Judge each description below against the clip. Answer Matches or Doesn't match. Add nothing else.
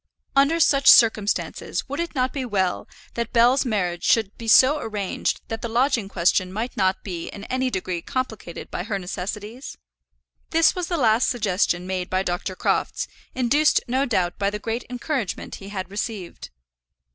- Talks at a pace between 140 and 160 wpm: Doesn't match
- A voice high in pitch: Matches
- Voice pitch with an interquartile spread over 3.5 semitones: Matches